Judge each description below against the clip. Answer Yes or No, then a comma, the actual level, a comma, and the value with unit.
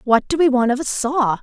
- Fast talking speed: Yes, fast, 295 wpm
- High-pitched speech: Yes, very high, 260 Hz